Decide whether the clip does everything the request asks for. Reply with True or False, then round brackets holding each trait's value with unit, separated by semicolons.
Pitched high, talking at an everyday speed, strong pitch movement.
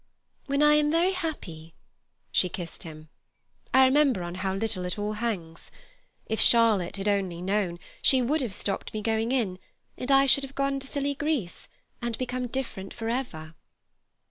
True (225 Hz; 165 wpm; 6.5 semitones)